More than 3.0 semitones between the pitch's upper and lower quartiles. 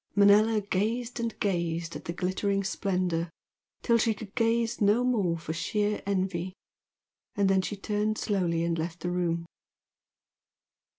Yes: average, 3.7 semitones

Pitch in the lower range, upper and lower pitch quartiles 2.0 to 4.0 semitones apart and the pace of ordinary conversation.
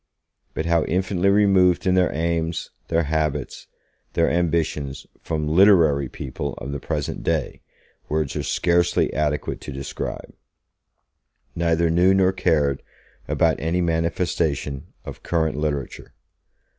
No: very low, 80 Hz; average, 2.8 semitones; slow, 120 wpm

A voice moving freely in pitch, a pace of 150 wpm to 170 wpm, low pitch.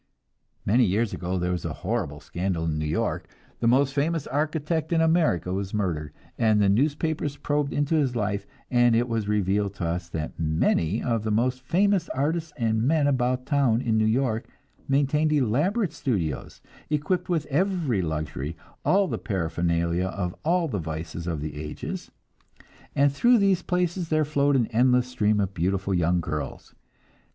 Yes: wide, 8.5 semitones; average, 165 wpm; low, 115 Hz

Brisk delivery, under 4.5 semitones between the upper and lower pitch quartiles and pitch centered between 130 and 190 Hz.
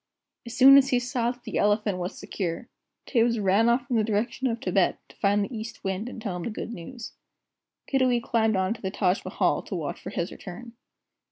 No: fast, 215 wpm; average, 3.3 semitones; high, 225 Hz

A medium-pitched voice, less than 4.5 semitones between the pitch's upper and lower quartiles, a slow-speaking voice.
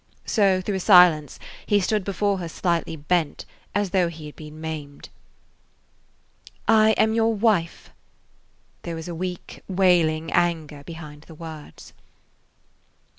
Yes: medium, 175 Hz; average, 3.7 semitones; slow, 130 wpm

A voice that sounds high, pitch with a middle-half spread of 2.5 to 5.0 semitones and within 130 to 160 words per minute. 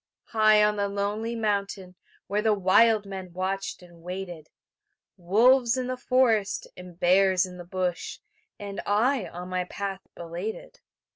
Yes: high, 200 Hz; average, 3.0 semitones; average, 145 wpm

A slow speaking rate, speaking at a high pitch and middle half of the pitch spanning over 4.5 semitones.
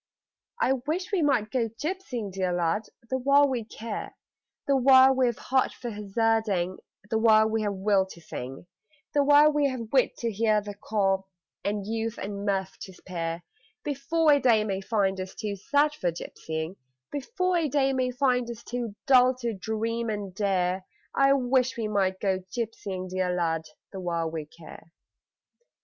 No: average, 165 wpm; high, 220 Hz; wide, 5.4 semitones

